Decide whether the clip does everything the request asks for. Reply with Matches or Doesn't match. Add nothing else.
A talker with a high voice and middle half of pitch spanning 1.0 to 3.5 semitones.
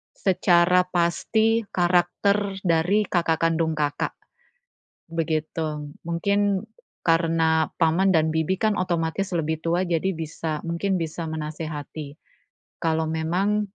Doesn't match